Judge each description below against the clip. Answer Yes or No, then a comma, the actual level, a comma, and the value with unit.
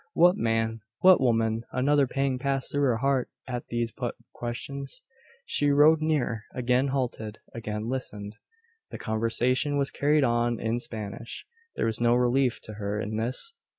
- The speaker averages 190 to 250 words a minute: No, average, 155 wpm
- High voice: No, low, 120 Hz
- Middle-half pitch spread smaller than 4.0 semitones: Yes, average, 3.5 semitones